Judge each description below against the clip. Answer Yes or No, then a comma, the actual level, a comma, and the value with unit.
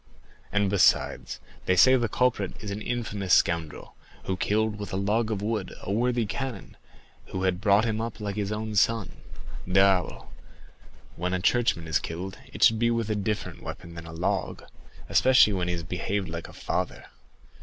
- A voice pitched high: No, low, 100 Hz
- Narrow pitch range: No, average, 3.2 semitones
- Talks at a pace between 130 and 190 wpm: Yes, average, 185 wpm